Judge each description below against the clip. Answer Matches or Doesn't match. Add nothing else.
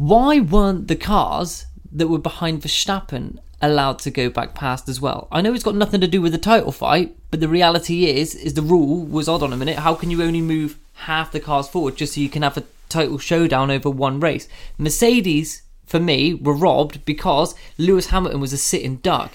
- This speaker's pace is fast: Matches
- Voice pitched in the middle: Matches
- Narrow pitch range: Doesn't match